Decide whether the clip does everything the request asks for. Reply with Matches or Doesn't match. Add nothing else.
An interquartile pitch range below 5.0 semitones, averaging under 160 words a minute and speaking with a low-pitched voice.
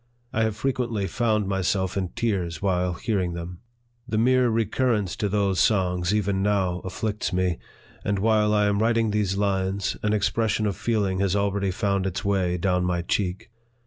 Doesn't match